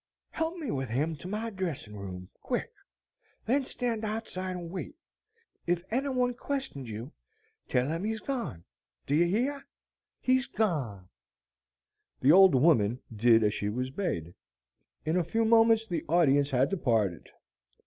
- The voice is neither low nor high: Yes, medium, 170 Hz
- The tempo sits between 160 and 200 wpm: No, average, 150 wpm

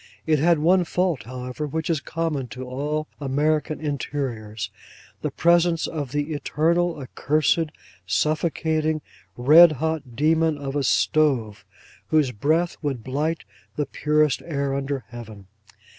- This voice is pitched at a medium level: Yes, medium, 150 Hz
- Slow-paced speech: Yes, slow, 130 wpm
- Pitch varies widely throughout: No, average, 3.0 semitones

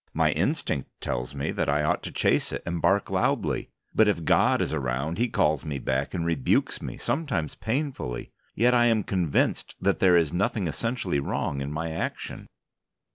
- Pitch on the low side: Yes, very low, 85 Hz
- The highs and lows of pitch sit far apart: Yes, wide, 6.3 semitones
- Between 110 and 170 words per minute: No, average, 185 wpm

